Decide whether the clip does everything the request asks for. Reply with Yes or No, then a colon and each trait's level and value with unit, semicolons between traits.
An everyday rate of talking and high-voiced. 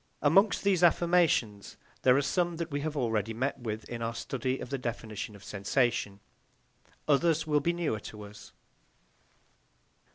No: average, 155 wpm; low, 130 Hz